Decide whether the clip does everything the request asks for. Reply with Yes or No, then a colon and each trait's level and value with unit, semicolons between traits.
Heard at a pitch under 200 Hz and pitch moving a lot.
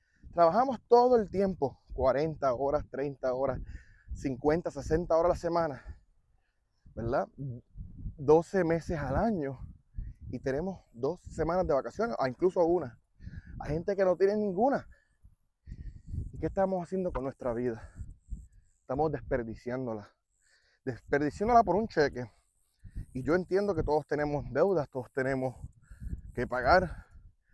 Yes: low, 135 Hz; wide, 8.5 semitones